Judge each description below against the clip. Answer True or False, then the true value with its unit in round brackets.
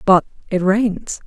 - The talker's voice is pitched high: True (195 Hz)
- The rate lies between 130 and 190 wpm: True (140 wpm)